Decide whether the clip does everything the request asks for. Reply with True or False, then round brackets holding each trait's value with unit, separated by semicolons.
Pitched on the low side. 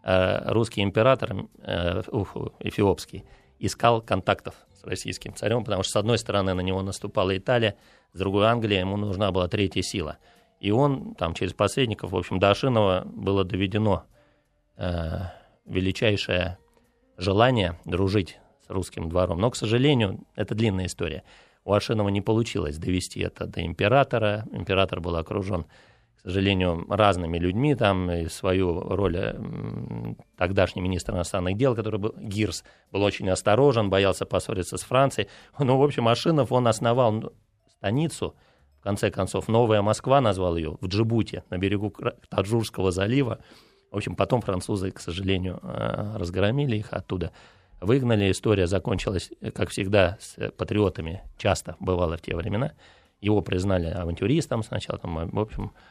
True (100 Hz)